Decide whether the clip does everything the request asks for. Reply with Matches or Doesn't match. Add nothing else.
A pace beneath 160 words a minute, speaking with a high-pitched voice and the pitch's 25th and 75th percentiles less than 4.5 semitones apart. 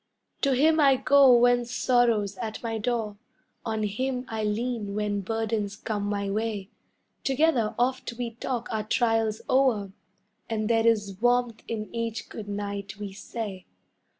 Matches